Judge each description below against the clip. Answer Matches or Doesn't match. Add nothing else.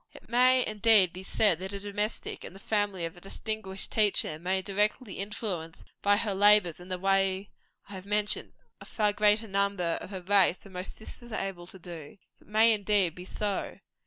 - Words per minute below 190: Doesn't match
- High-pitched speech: Matches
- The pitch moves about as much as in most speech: Doesn't match